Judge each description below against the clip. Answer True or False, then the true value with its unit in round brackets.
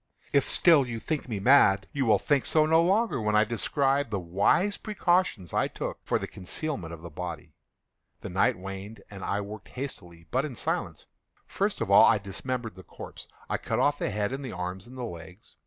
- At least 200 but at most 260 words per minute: True (205 wpm)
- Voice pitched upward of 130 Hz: False (110 Hz)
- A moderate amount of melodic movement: False (6.6 semitones)